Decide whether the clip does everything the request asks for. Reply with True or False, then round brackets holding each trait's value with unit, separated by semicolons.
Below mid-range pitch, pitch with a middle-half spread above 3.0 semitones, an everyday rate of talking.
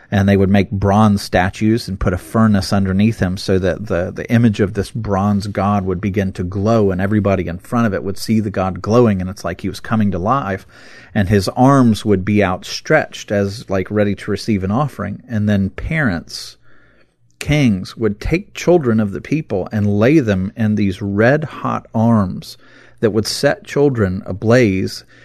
False (105 Hz; 2.6 semitones; 190 wpm)